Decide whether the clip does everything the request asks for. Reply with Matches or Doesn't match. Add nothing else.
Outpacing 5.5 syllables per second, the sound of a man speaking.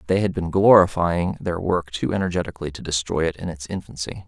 Matches